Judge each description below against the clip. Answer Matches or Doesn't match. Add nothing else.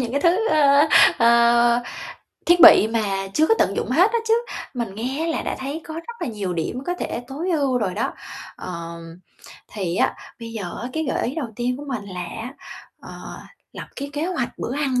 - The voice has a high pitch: Matches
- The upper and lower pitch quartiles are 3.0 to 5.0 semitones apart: Doesn't match